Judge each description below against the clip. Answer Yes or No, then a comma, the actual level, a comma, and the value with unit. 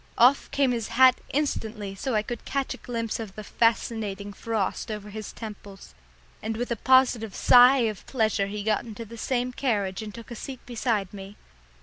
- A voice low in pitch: No, high, 225 Hz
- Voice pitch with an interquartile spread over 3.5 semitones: No, average, 2.9 semitones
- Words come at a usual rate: Yes, average, 190 wpm